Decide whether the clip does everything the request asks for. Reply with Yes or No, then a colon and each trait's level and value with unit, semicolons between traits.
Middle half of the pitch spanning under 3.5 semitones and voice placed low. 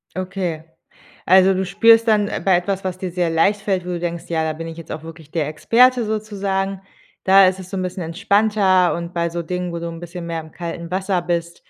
No: narrow, 2.5 semitones; medium, 180 Hz